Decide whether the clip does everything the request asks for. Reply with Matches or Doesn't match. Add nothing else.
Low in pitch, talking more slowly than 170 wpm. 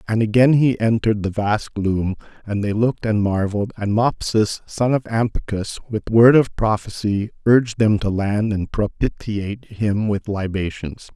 Matches